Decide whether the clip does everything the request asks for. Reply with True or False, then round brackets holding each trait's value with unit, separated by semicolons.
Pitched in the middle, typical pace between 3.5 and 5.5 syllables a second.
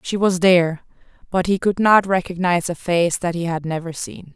True (175 Hz; 5.3 syllables/s)